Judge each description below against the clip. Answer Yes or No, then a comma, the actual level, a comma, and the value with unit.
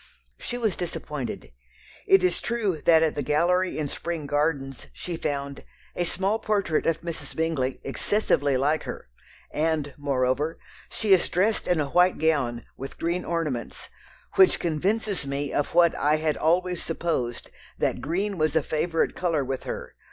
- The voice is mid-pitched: Yes, medium, 160 Hz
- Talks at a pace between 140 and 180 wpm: Yes, average, 160 wpm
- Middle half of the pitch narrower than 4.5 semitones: Yes, average, 3.8 semitones